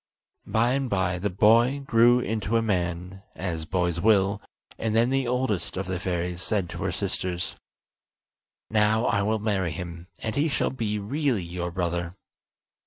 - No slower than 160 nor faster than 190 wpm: Yes, average, 165 wpm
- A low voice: Yes, low, 100 Hz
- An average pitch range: Yes, average, 4.1 semitones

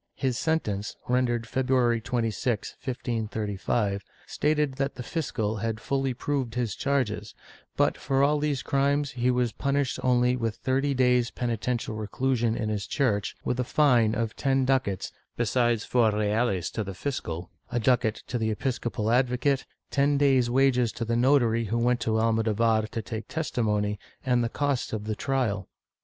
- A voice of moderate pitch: No, low, 120 Hz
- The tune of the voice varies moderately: Yes, average, 3.2 semitones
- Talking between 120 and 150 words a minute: No, average, 160 wpm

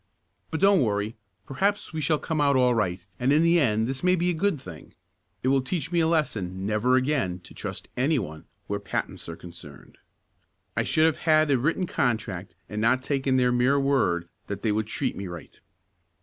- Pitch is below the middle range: Yes, low, 130 Hz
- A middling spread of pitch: No, wide, 7.2 semitones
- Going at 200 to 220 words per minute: Yes, fast, 205 wpm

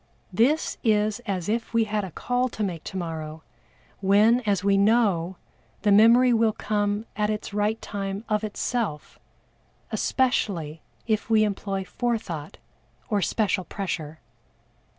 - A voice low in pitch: No, high, 205 Hz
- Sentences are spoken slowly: Yes, slow, 130 wpm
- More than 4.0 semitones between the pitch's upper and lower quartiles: No, average, 2.8 semitones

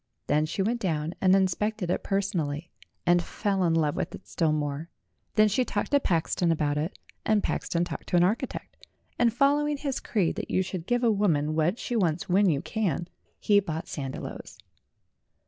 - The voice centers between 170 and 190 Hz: Yes, medium, 185 Hz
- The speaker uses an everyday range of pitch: Yes, average, 4.8 semitones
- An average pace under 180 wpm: No, average, 190 wpm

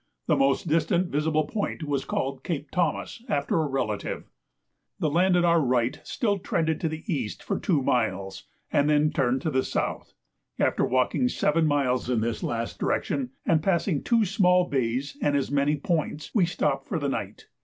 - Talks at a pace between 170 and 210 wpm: Yes, average, 180 wpm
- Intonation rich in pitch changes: No, average, 4.3 semitones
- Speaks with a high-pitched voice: No, medium, 150 Hz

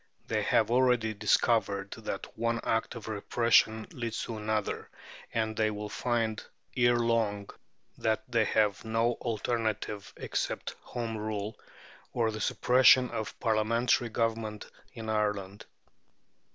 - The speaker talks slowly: Yes, slow, 125 wpm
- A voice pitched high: No, low, 110 Hz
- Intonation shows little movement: Yes, narrow, 1.6 semitones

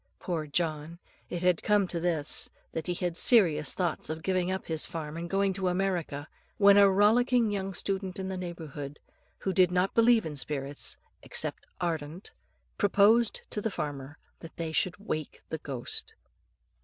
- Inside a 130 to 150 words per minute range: No, average, 165 wpm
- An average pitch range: Yes, average, 3.7 semitones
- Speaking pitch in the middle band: Yes, medium, 180 Hz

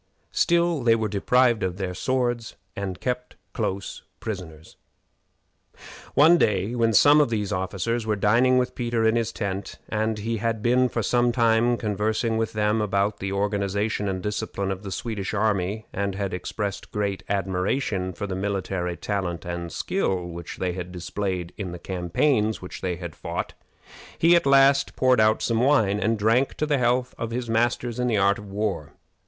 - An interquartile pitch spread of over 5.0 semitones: No, average, 3.6 semitones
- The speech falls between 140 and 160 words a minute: No, average, 175 wpm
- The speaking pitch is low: Yes, low, 105 Hz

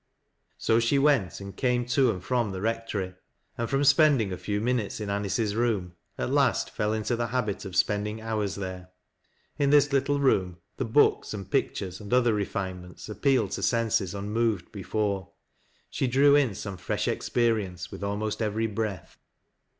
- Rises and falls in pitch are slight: No, average, 3.6 semitones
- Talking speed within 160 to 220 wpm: Yes, average, 180 wpm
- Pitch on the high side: No, low, 110 Hz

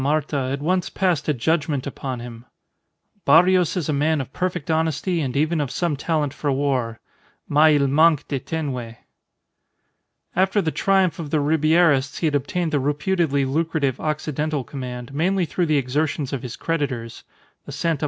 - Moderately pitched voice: Yes, medium, 150 Hz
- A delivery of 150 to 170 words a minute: Yes, average, 165 wpm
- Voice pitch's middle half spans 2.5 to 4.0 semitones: Yes, average, 3.2 semitones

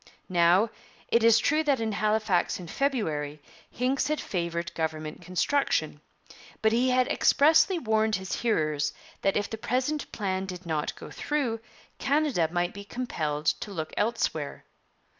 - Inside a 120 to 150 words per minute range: Yes, average, 145 wpm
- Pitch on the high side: Yes, high, 215 Hz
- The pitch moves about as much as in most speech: No, wide, 6.8 semitones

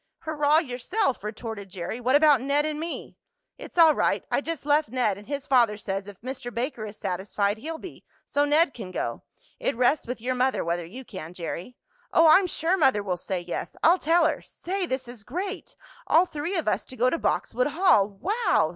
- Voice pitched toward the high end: Yes, very high, 260 Hz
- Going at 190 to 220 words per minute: Yes, fast, 205 wpm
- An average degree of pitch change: No, wide, 7.2 semitones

